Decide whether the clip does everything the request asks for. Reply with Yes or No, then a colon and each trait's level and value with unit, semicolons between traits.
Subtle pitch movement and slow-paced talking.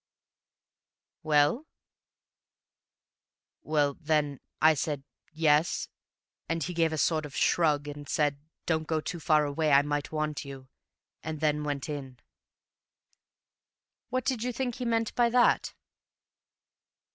Yes: narrow, 2.2 semitones; slow, 125 wpm